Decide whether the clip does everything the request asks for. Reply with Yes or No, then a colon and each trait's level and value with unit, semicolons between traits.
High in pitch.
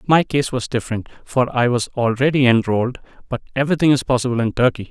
No: low, 125 Hz